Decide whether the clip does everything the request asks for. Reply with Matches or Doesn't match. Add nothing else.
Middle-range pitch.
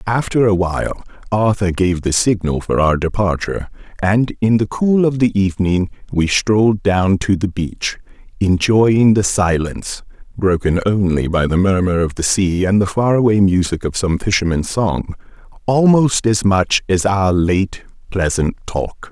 Doesn't match